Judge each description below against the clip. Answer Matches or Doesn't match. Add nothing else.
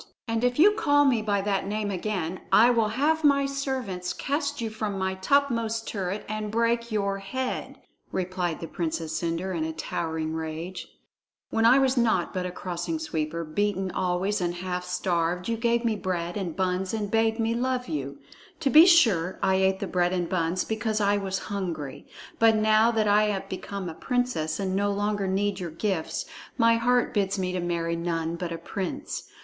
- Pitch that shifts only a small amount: Doesn't match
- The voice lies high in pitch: Matches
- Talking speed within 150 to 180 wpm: Doesn't match